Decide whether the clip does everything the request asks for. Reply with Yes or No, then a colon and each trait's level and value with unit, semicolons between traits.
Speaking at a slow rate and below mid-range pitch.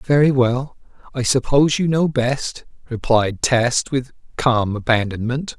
Yes: slow, 130 wpm; low, 125 Hz